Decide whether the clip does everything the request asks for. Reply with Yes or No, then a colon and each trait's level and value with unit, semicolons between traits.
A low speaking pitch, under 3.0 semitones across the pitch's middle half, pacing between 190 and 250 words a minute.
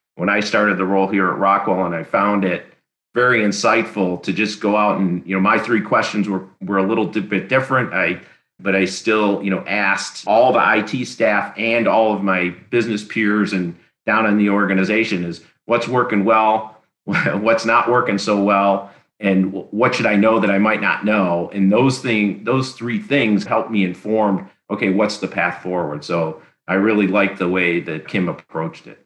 Yes: low, 100 Hz; narrow, 2.4 semitones; average, 195 wpm